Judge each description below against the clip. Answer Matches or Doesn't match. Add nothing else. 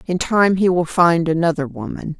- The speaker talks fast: Doesn't match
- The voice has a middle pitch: Matches